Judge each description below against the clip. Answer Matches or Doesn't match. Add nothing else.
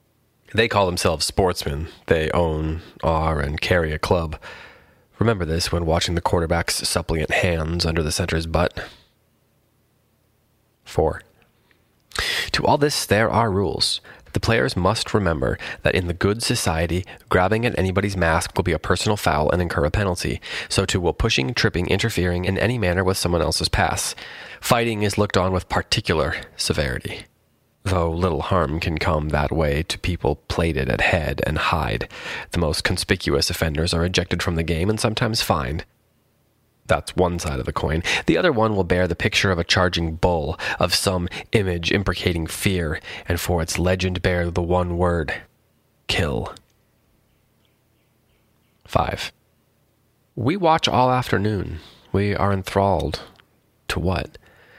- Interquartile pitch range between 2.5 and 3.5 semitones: Doesn't match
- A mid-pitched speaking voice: Doesn't match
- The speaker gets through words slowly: Doesn't match